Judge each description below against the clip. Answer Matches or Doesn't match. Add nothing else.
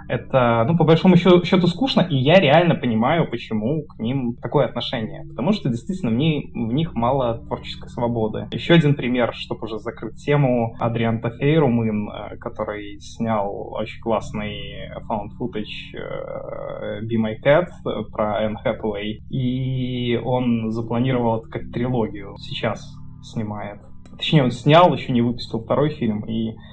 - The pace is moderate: Matches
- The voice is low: Matches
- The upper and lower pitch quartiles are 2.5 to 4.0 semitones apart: Doesn't match